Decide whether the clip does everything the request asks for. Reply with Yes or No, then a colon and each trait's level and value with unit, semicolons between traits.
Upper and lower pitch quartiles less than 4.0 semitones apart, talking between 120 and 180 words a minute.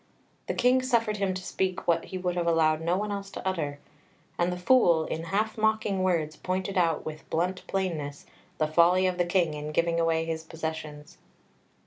No: average, 2.9 semitones; average, 190 wpm